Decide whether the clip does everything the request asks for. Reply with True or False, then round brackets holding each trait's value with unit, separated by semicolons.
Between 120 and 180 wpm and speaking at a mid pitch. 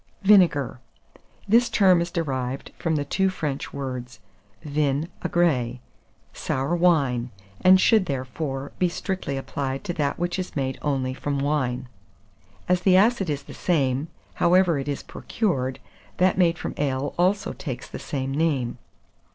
True (145 wpm; 145 Hz)